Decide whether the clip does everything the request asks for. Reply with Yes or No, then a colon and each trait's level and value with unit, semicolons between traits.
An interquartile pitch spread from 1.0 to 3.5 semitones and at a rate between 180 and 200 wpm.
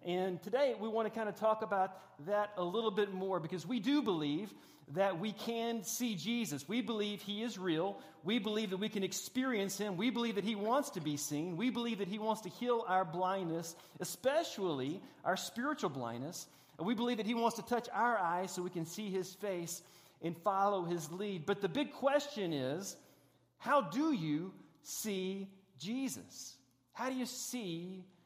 No: average, 4.5 semitones; average, 190 wpm